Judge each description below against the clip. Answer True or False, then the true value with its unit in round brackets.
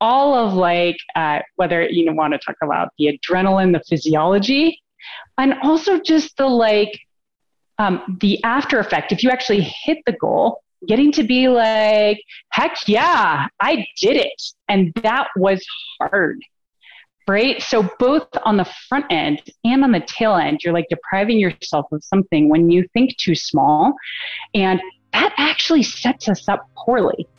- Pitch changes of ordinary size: False (6.4 semitones)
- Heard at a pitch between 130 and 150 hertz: False (215 Hz)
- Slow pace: False (160 wpm)